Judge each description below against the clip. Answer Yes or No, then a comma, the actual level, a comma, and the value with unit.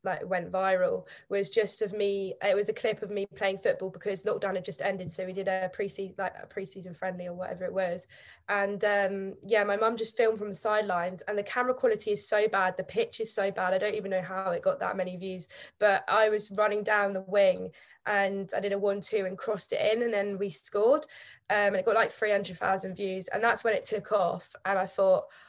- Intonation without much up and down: Yes, narrow, 2.0 semitones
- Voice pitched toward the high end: Yes, high, 200 Hz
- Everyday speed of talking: No, fast, 245 wpm